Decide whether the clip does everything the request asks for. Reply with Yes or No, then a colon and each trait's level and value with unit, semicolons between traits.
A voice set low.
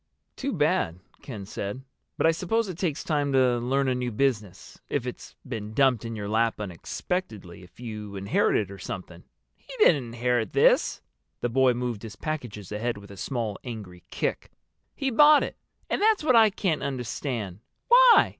Yes: low, 120 Hz